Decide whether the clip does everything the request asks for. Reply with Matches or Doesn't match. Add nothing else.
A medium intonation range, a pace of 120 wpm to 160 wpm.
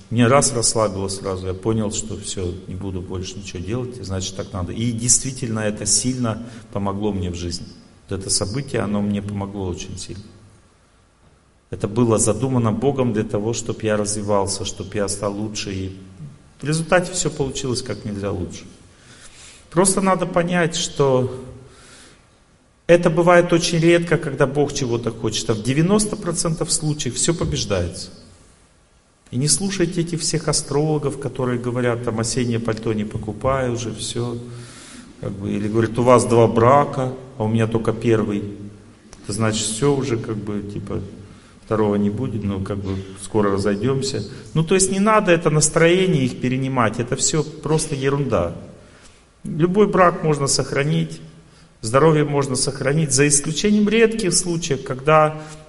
Doesn't match